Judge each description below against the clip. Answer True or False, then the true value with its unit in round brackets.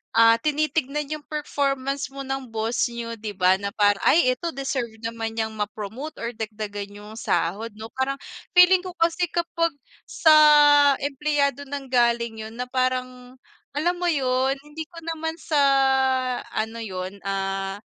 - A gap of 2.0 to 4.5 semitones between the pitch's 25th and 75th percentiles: False (5.0 semitones)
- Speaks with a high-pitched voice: True (255 Hz)